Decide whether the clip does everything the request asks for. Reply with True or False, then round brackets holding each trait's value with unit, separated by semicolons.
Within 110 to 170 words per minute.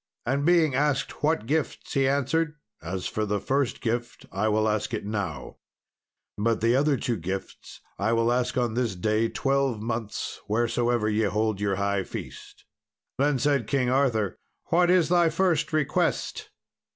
True (160 wpm)